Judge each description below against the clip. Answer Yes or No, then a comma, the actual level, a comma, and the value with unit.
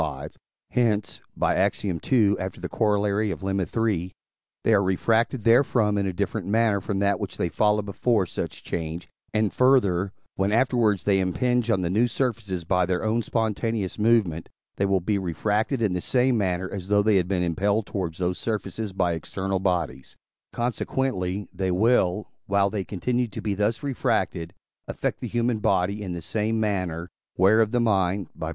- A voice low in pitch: Yes, low, 100 Hz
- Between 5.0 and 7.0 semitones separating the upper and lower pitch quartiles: No, average, 3.4 semitones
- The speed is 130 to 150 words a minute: No, average, 175 wpm